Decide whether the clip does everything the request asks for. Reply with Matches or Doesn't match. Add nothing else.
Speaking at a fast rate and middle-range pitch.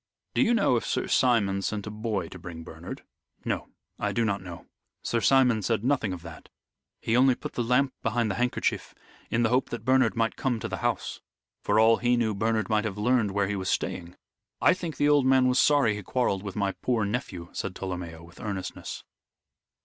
Doesn't match